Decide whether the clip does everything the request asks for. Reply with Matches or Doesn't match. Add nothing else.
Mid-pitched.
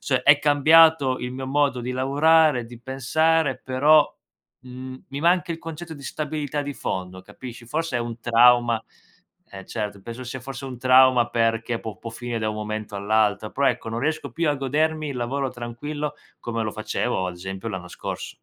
Doesn't match